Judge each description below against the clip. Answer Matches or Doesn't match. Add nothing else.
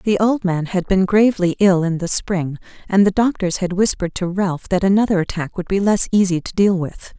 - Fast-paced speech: Matches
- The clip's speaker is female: Matches